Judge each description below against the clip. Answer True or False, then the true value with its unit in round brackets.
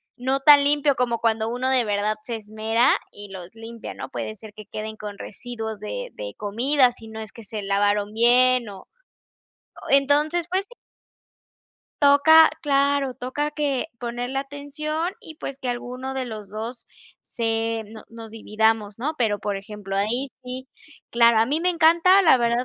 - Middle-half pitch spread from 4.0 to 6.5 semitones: True (4.4 semitones)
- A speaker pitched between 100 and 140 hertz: False (240 Hz)